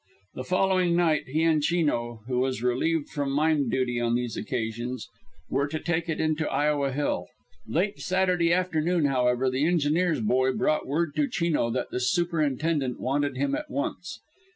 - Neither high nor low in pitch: Yes, medium, 150 Hz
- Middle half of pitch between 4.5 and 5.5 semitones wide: Yes, average, 4.8 semitones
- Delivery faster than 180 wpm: No, average, 170 wpm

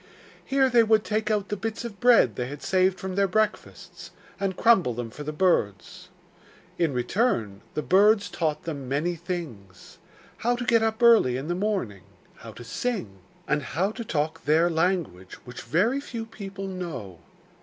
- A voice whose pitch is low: No, medium, 180 Hz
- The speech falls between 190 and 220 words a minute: No, average, 175 wpm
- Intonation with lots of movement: Yes, wide, 7.6 semitones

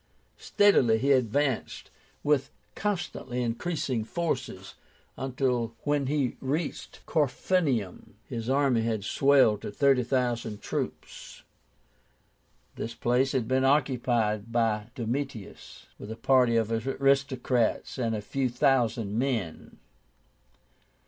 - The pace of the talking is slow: Yes, slow, 105 wpm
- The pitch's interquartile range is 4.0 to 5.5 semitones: No, average, 3.3 semitones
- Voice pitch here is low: Yes, low, 125 Hz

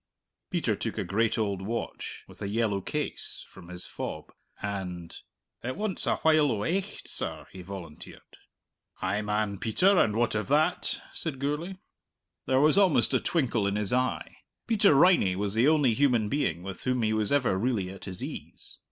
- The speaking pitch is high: No, low, 110 Hz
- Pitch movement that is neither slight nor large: No, wide, 6.4 semitones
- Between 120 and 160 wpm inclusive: No, average, 180 wpm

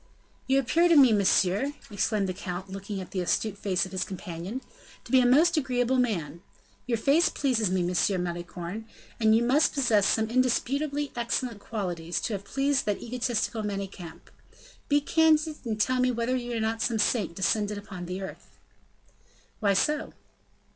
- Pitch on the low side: No, high, 220 Hz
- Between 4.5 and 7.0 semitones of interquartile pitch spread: Yes, average, 5.1 semitones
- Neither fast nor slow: Yes, average, 170 wpm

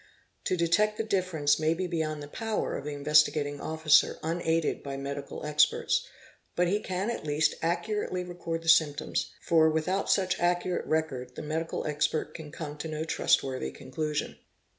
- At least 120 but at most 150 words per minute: No, average, 165 wpm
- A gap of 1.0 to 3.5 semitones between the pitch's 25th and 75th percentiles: Yes, average, 2.9 semitones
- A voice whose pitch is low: No, medium, 160 Hz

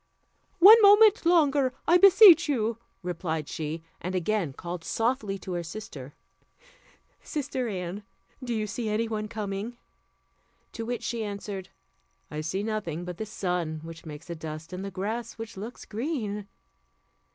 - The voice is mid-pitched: No, high, 210 Hz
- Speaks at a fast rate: No, average, 150 wpm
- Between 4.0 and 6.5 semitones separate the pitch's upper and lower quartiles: Yes, wide, 5.4 semitones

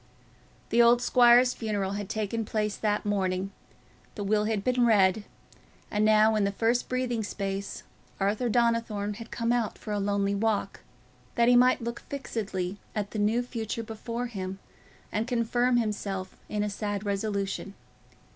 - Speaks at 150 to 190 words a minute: Yes, average, 155 wpm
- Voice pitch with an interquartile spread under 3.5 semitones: Yes, narrow, 2.6 semitones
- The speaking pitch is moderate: No, high, 215 Hz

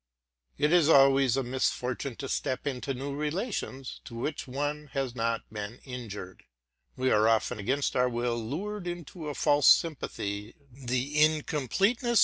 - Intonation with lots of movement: No, average, 3.6 semitones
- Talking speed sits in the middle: Yes, average, 145 wpm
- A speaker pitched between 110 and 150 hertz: Yes, low, 135 Hz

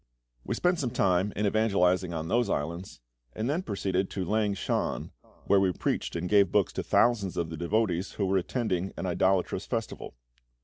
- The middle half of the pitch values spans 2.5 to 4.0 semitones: Yes, average, 3.3 semitones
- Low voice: Yes, very low, 95 Hz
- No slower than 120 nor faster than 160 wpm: No, average, 180 wpm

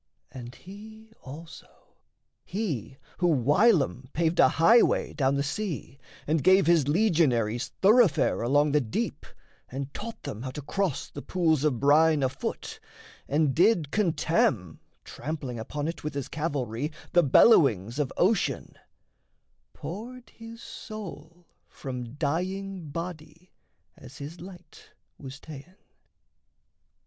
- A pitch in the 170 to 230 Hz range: No, medium, 155 Hz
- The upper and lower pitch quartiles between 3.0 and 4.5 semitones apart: No, average, 5.2 semitones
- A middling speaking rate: No, slow, 120 wpm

